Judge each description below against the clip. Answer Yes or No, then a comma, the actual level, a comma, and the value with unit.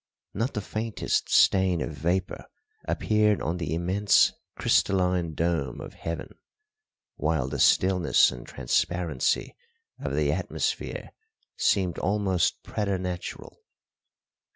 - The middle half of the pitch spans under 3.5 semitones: Yes, average, 3.1 semitones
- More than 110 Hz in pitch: No, very low, 90 Hz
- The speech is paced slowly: Yes, slow, 105 wpm